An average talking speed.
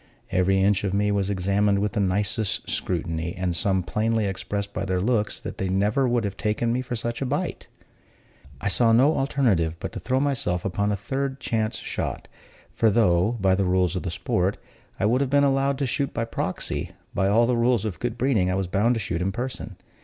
No: fast, 215 wpm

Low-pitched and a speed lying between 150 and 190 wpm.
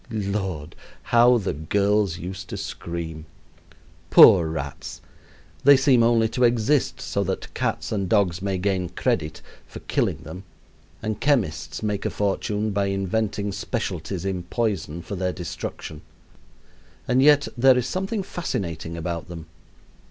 No: low, 100 Hz; slow, 135 wpm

